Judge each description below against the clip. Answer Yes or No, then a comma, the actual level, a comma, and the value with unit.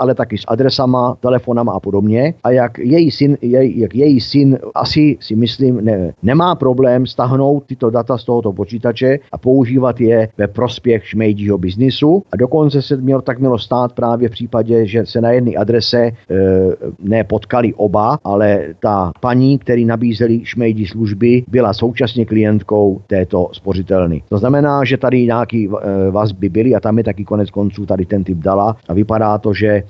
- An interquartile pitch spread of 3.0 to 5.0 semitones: Yes, average, 3.4 semitones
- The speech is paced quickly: Yes, fast, 175 wpm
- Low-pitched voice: Yes, low, 115 Hz